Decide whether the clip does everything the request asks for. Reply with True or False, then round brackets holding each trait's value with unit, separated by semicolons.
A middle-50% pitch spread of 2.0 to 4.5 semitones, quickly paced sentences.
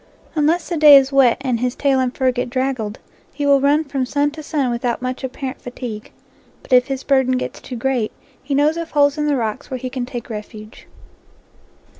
True (2.5 semitones; 210 wpm)